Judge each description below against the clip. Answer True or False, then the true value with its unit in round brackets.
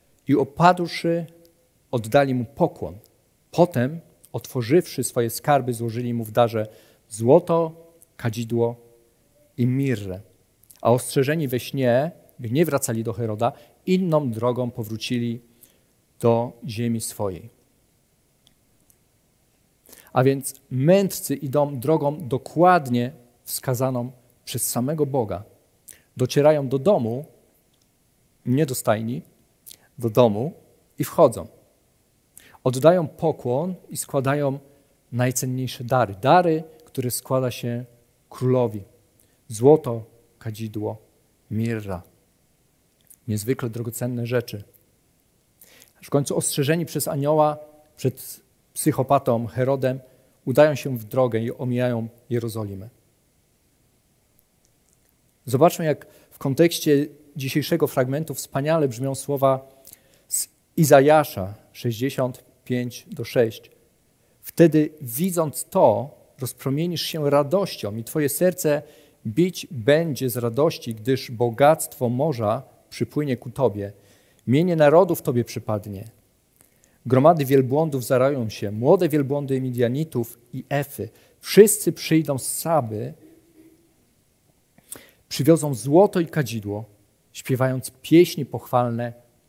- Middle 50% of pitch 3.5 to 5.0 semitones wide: True (4.1 semitones)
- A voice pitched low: True (130 Hz)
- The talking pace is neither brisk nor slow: False (90 wpm)